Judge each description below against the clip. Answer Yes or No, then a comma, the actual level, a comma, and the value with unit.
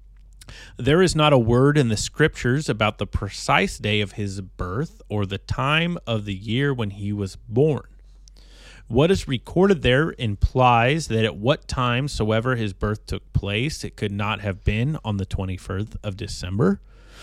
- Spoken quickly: No, average, 175 wpm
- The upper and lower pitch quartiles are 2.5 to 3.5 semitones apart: No, average, 4.9 semitones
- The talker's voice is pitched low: Yes, low, 110 Hz